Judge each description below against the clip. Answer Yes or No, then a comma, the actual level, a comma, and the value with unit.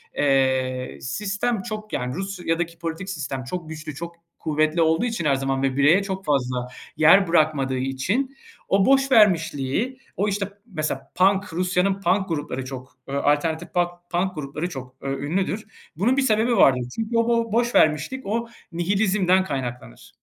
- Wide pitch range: Yes, wide, 6.1 semitones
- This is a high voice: No, medium, 170 Hz